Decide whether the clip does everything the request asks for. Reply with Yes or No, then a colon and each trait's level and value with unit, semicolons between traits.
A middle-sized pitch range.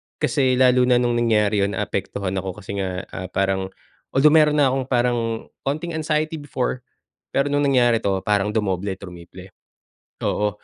No: wide, 5.7 semitones